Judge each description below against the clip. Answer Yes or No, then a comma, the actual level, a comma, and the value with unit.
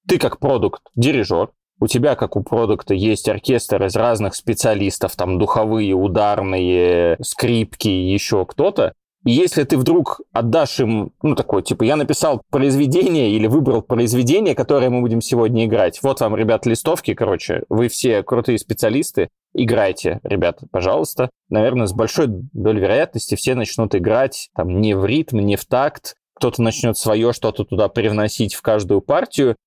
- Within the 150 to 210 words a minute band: Yes, average, 155 wpm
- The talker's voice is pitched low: Yes, low, 110 Hz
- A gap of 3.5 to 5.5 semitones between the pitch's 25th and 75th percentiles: No, average, 2.9 semitones